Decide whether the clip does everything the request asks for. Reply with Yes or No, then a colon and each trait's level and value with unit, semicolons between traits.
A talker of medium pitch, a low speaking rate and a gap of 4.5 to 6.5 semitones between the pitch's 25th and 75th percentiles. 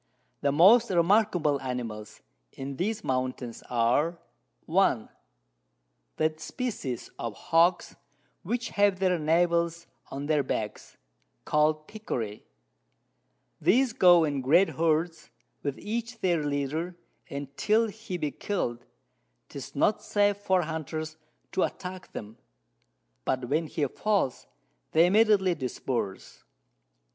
Yes: medium, 165 Hz; slow, 115 wpm; wide, 5.5 semitones